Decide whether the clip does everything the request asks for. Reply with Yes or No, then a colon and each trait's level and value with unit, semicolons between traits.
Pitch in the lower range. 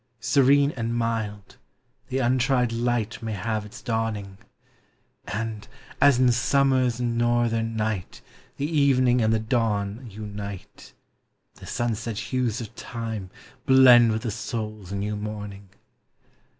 Yes: low, 115 Hz